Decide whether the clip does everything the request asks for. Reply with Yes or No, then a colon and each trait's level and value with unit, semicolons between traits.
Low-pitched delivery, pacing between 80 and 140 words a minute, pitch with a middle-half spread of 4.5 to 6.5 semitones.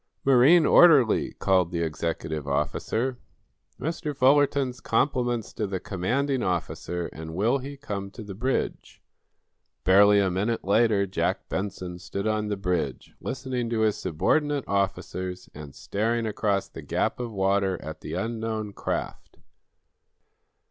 Yes: low, 105 Hz; slow, 135 wpm; average, 5.1 semitones